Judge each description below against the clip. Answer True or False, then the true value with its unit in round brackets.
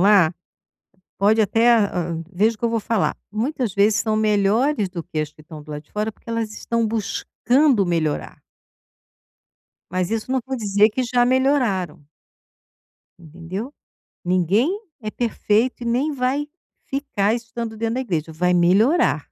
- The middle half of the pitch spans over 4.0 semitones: True (4.7 semitones)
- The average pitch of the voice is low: False (215 Hz)